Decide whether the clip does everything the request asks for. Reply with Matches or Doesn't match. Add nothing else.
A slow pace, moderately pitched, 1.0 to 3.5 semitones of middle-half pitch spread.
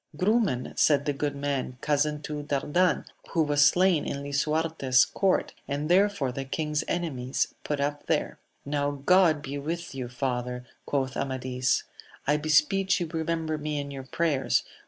Doesn't match